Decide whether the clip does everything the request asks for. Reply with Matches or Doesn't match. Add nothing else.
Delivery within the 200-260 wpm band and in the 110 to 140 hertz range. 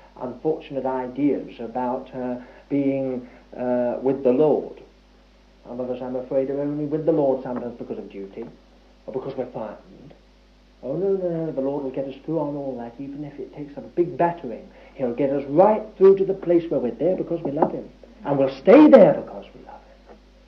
Matches